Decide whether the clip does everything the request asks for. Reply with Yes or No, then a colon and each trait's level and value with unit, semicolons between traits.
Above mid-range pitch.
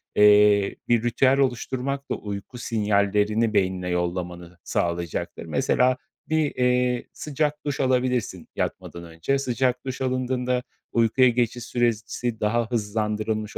No: low, 115 Hz